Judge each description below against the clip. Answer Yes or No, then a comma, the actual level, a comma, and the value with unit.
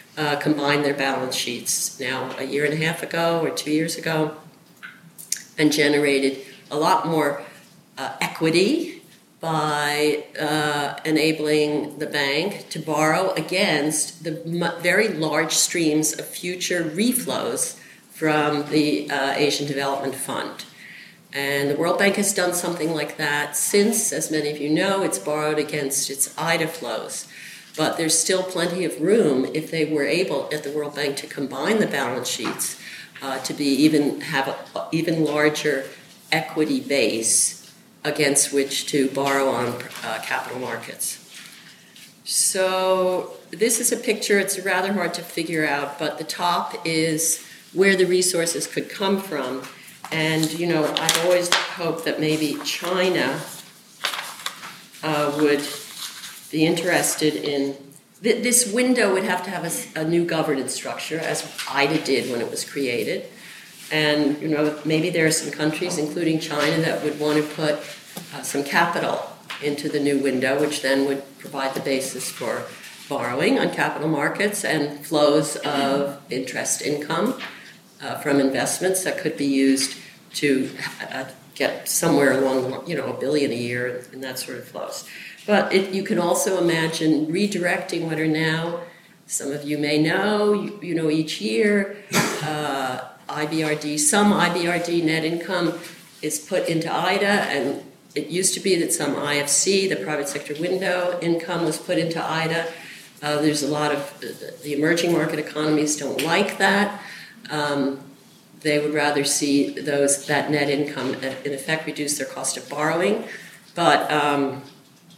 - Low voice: No, medium, 155 Hz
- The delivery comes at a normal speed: Yes, average, 155 wpm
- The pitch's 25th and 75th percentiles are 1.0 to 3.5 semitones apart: Yes, average, 3.2 semitones